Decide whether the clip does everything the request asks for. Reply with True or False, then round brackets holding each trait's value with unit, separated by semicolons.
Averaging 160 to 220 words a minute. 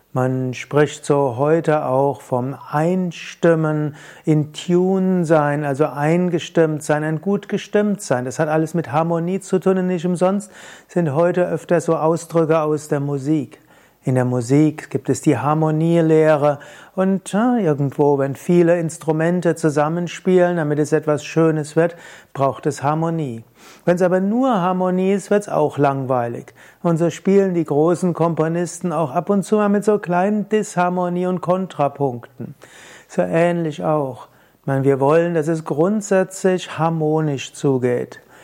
False (150 wpm)